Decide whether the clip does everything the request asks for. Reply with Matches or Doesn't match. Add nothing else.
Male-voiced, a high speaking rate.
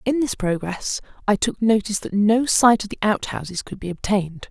Doesn't match